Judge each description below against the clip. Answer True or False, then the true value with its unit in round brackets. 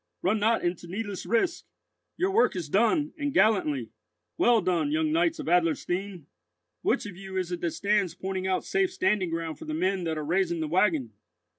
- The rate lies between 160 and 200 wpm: True (190 wpm)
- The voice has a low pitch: False (190 Hz)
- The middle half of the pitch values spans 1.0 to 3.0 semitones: False (5.1 semitones)